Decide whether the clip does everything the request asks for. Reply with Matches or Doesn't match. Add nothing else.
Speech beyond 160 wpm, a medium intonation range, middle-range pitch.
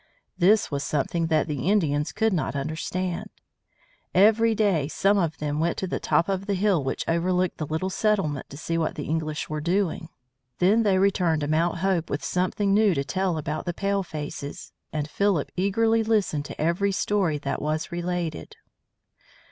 Matches